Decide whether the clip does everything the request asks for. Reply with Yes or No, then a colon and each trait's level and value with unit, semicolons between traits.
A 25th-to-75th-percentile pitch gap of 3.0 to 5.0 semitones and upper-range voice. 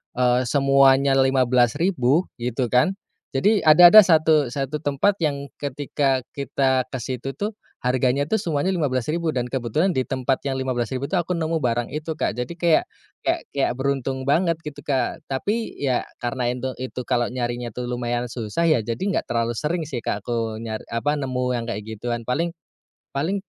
No: average, 3.6 semitones; low, 130 Hz